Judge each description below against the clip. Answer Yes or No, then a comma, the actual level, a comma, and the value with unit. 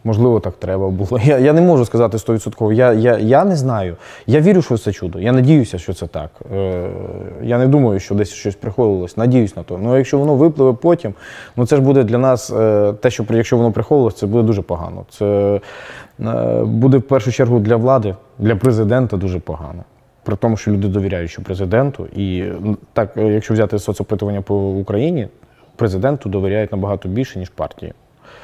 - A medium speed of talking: No, fast, 190 wpm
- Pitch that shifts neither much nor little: Yes, average, 4.1 semitones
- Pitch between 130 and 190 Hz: No, low, 110 Hz